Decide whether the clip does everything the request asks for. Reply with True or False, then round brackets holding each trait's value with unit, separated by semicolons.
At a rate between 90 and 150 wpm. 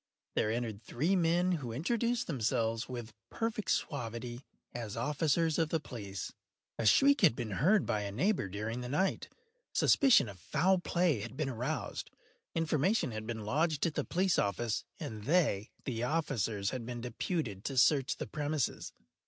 False (160 wpm)